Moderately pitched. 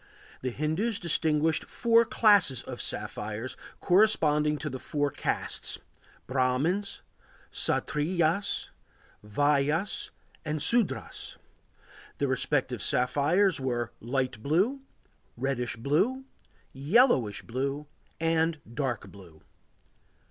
Yes: medium, 150 Hz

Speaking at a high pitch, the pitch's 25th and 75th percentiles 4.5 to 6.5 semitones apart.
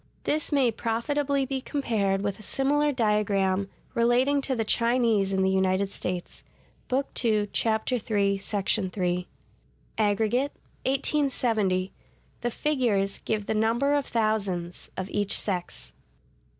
Yes: high, 220 Hz; average, 4.8 semitones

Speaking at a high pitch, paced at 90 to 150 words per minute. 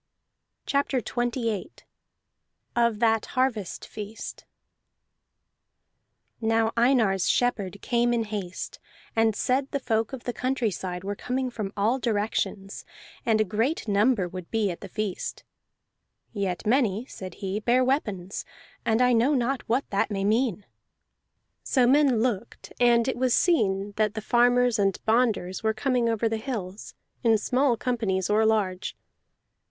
Yes: high, 225 Hz; average, 140 wpm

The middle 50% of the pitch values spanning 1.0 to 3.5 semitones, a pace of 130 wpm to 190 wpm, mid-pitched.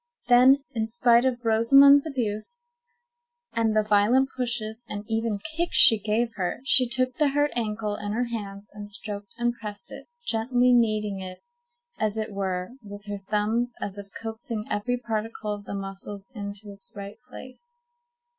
No: average, 3.0 semitones; average, 165 wpm; high, 220 Hz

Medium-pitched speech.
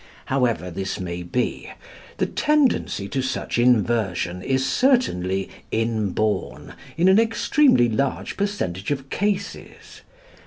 No: low, 120 Hz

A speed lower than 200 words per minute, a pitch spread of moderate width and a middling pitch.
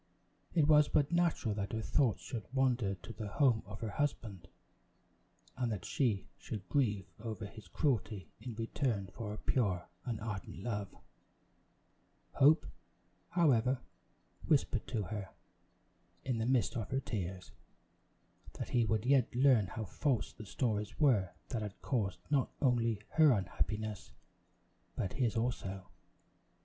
No: average, 140 wpm; average, 4.0 semitones; low, 115 Hz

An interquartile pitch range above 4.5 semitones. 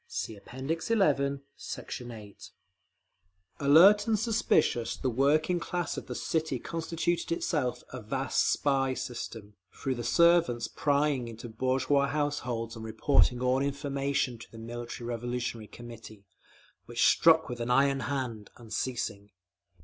No: average, 3.8 semitones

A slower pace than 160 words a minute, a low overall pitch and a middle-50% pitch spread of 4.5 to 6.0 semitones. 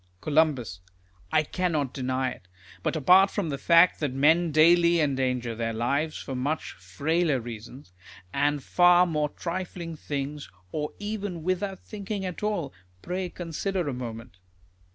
No: average, 140 wpm; medium, 155 Hz; average, 4.9 semitones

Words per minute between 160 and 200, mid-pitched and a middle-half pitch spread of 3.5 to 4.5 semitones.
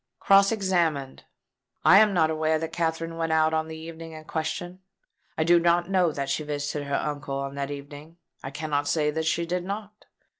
No: average, 195 wpm; medium, 160 Hz; average, 2.7 semitones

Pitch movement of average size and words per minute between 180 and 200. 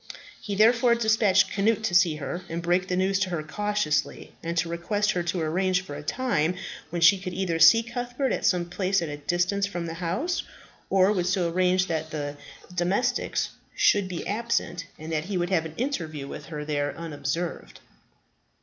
Yes: average, 3.6 semitones; average, 190 wpm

